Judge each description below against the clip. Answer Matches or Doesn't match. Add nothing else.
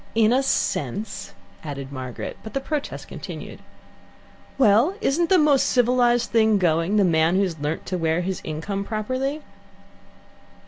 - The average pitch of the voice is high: Matches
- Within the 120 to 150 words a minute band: Matches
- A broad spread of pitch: Matches